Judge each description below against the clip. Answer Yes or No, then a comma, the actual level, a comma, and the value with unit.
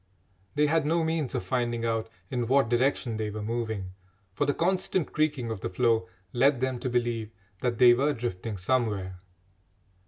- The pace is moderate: Yes, average, 175 wpm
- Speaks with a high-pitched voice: No, low, 120 Hz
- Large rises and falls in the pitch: No, average, 3.7 semitones